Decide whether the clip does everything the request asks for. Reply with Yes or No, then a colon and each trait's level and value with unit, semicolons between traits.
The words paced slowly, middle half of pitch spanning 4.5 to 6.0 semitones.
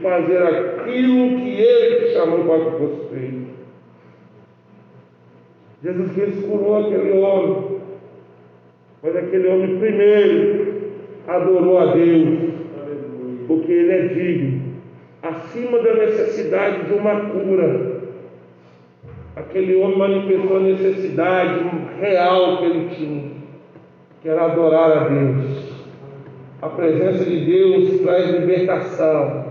Yes: slow, 100 wpm; average, 5.1 semitones